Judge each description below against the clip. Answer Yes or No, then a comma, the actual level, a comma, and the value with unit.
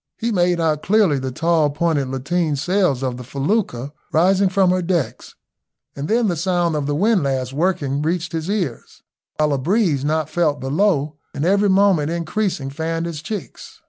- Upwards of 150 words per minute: Yes, average, 175 wpm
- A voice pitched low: No, medium, 165 Hz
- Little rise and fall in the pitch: No, average, 4.4 semitones